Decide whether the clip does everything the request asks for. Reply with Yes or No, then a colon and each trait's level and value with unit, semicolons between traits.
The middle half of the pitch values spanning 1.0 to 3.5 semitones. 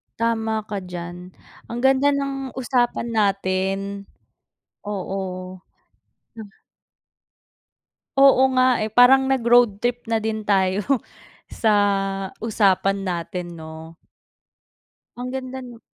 No: average, 4.3 semitones